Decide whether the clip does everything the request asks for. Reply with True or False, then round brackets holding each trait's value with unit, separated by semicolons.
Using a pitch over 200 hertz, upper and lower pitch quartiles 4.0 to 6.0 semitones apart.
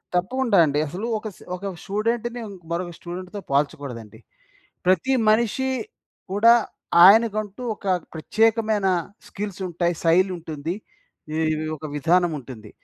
False (190 Hz; 4.8 semitones)